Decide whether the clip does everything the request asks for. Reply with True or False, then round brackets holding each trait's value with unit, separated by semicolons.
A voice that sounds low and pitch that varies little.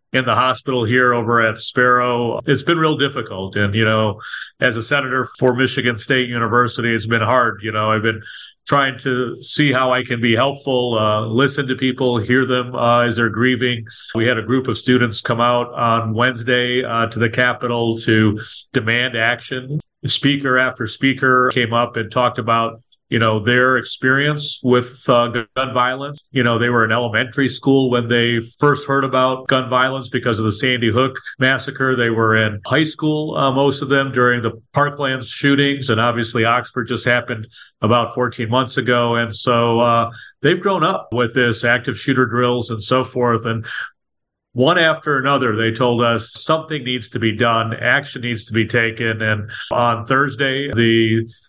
True (125 Hz; 2.2 semitones)